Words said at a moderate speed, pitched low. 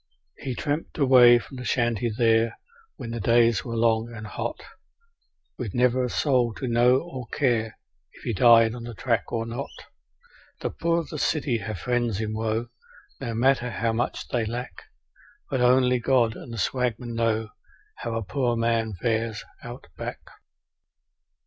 Yes: average, 165 wpm; low, 120 Hz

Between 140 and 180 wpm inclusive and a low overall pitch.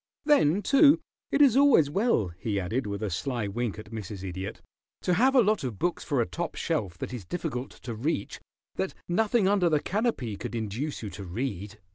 No: average, 200 wpm; low, 130 Hz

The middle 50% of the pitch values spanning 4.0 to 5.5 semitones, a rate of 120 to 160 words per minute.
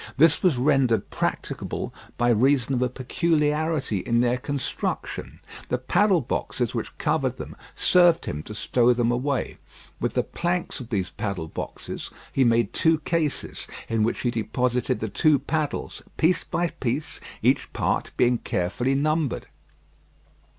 Yes: average, 4.6 semitones; average, 145 wpm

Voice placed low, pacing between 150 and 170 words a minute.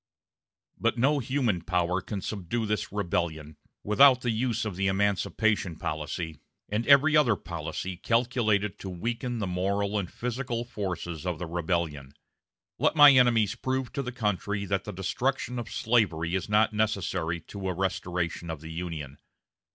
Yes: low, 100 Hz; average, 155 wpm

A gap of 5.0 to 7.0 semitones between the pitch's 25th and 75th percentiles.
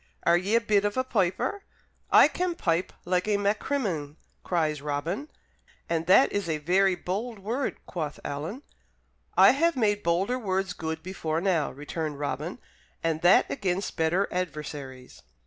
No: average, 4.5 semitones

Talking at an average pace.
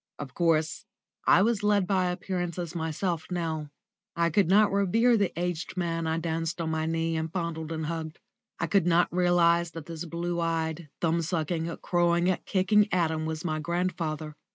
Yes: average, 170 wpm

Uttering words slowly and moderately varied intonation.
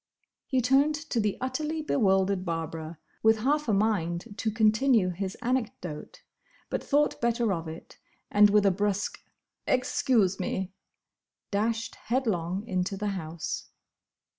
Yes: slow, 130 wpm; average, 4.7 semitones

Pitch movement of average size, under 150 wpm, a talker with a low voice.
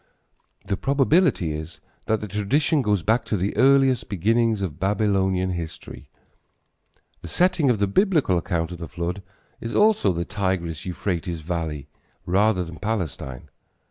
Yes: average, 4.9 semitones; average, 140 wpm; low, 100 Hz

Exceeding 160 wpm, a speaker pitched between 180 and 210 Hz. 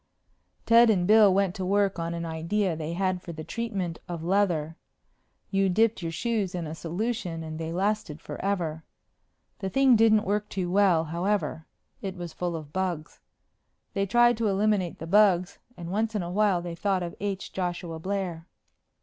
Yes: average, 175 wpm; medium, 185 Hz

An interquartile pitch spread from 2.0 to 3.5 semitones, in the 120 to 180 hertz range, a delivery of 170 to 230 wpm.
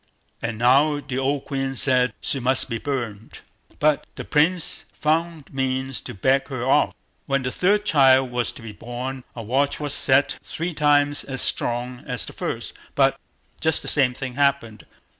Yes: narrow, 2.6 semitones; low, 135 Hz; average, 180 wpm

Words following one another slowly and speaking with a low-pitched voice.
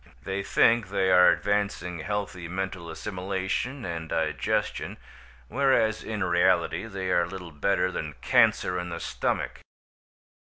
Yes: slow, 125 wpm; very low, 95 Hz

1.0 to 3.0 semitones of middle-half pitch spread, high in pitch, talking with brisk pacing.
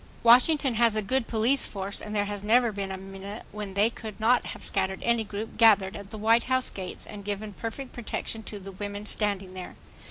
Yes: narrow, 2.6 semitones; high, 210 Hz; fast, 215 wpm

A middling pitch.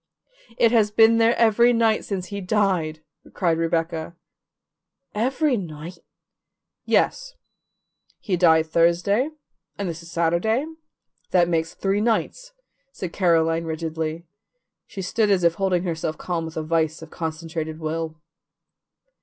Yes: medium, 175 Hz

